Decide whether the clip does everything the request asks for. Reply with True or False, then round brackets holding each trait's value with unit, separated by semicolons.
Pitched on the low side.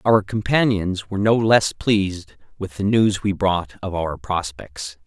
True (100 Hz)